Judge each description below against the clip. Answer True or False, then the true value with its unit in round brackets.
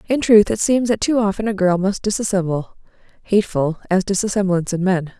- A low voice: False (200 Hz)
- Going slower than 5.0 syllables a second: False (5.4 syllables/s)